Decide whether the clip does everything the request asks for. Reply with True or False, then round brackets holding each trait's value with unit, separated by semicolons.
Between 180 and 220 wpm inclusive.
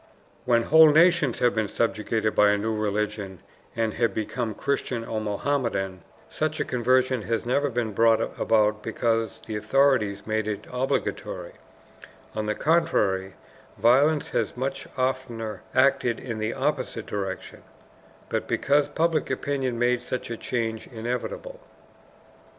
False (135 wpm)